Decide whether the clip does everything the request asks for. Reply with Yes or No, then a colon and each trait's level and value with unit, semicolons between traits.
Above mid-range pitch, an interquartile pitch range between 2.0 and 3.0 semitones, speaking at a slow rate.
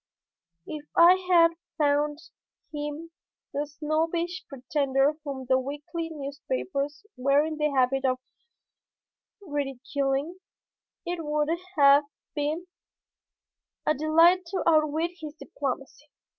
Yes: very high, 295 Hz; average, 2.7 semitones; slow, 105 wpm